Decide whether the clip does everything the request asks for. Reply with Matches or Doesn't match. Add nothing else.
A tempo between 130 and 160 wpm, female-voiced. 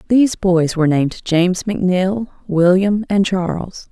Matches